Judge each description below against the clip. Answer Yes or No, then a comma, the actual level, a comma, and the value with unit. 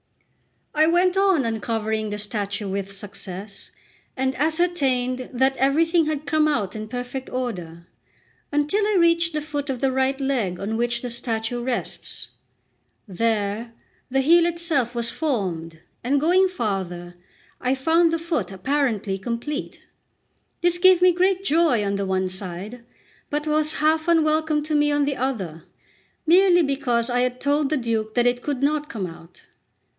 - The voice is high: Yes, very high, 260 Hz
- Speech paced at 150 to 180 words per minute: Yes, average, 155 wpm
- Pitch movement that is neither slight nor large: No, wide, 6.2 semitones